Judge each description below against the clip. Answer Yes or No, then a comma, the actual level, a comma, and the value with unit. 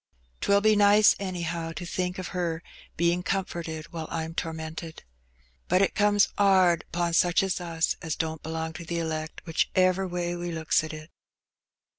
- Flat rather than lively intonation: Yes, narrow, 2.2 semitones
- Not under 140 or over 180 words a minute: Yes, average, 170 wpm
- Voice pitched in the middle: Yes, medium, 170 Hz